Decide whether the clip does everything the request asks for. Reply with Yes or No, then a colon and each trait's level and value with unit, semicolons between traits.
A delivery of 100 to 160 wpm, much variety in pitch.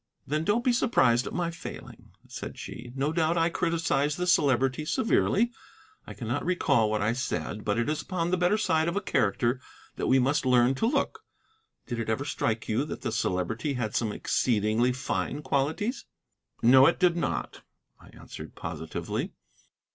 No: average, 175 wpm; wide, 6.2 semitones